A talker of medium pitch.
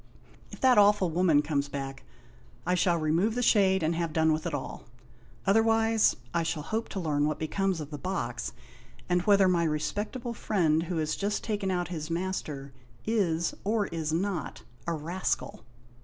Yes: medium, 175 Hz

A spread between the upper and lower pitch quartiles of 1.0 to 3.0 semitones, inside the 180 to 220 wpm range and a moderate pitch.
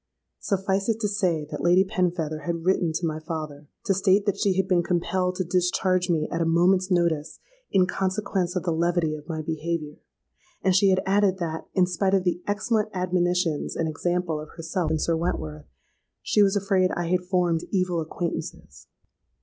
Yes: narrow, 2.6 semitones; average, 185 wpm; medium, 180 Hz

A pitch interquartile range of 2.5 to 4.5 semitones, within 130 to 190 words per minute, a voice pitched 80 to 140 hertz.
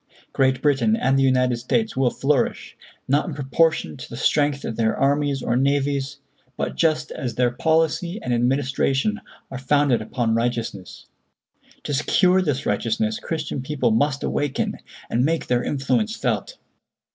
Yes: average, 3.4 semitones; average, 150 wpm; low, 135 Hz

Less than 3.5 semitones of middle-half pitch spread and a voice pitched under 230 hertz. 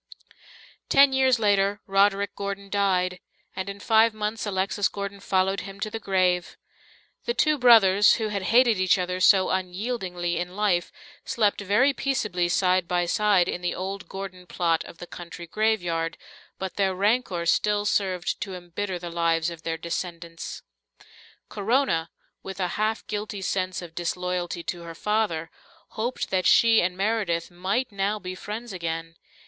Yes: average, 3.0 semitones; high, 190 Hz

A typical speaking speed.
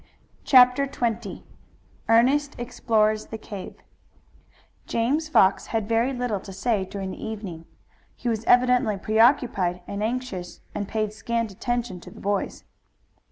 No: slow, 130 wpm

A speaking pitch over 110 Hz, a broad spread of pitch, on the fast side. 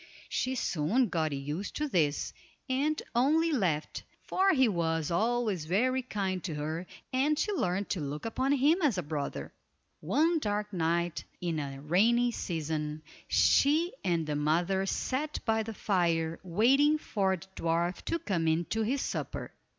No: high, 190 Hz; wide, 7.9 semitones; average, 160 wpm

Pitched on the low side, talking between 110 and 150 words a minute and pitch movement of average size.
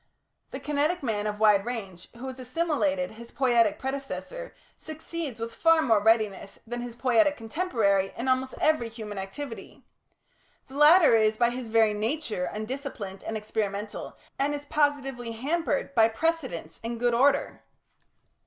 No: high, 240 Hz; average, 145 wpm; average, 4.8 semitones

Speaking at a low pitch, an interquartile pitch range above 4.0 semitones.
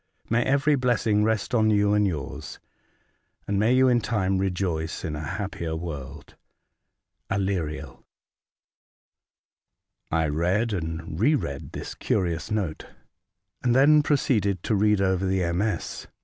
Yes: low, 100 Hz; average, 4.8 semitones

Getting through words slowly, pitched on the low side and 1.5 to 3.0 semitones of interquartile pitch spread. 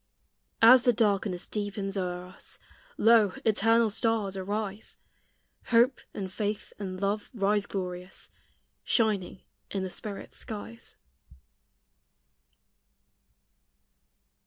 No: slow, 90 wpm; high, 205 Hz; narrow, 2.5 semitones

